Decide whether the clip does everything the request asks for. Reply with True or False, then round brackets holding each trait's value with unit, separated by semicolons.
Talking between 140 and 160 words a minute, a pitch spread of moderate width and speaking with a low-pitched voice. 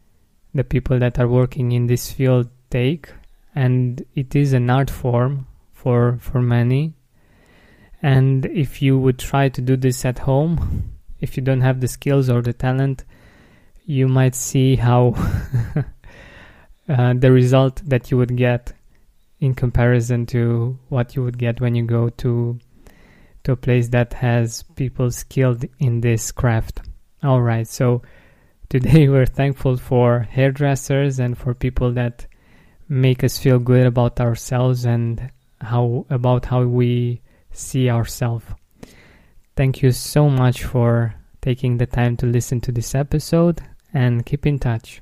False (150 wpm; 1.6 semitones; 125 Hz)